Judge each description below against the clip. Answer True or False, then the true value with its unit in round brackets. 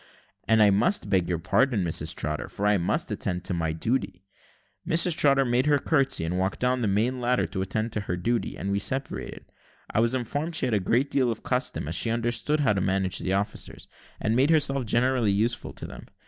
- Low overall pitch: True (115 Hz)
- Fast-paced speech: True (215 wpm)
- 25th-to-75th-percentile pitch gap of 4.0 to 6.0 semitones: True (5.1 semitones)